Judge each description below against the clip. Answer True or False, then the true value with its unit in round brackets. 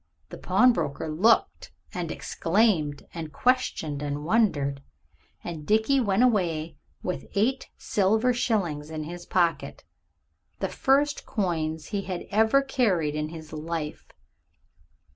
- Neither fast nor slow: False (120 wpm)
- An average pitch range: False (6.2 semitones)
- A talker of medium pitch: True (175 Hz)